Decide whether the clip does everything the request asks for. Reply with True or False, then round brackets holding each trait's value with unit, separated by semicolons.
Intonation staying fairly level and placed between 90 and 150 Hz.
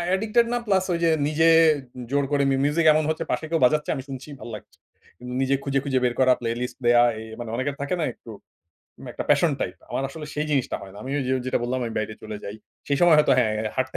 False (3.9 semitones; 135 Hz)